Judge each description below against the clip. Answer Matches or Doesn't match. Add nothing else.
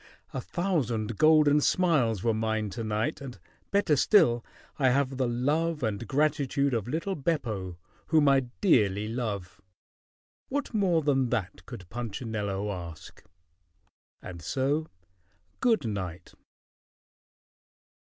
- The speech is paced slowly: Matches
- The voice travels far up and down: Matches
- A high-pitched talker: Doesn't match